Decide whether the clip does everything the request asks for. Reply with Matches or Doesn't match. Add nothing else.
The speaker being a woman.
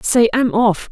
Matches